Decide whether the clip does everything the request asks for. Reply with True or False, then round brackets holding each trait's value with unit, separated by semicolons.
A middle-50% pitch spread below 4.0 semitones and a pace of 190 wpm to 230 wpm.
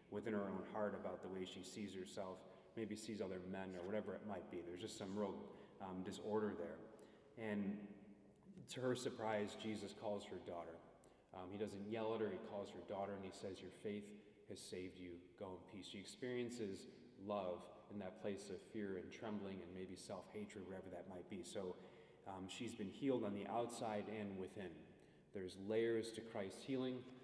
True (2.6 semitones; 195 wpm)